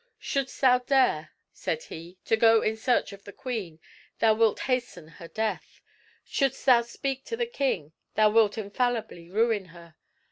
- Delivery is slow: No, average, 165 wpm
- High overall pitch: Yes, high, 225 Hz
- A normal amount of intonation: Yes, average, 4.2 semitones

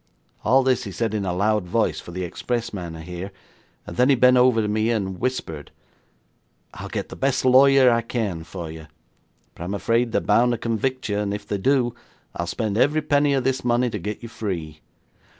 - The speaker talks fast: Yes, fast, 210 wpm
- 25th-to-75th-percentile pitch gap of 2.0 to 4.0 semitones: No, average, 4.9 semitones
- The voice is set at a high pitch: No, low, 110 Hz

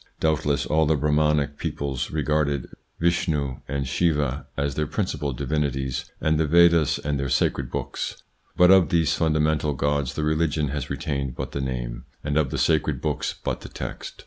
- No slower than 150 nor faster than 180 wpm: Yes, average, 170 wpm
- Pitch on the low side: Yes, very low, 75 Hz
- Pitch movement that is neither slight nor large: No, narrow, 2.1 semitones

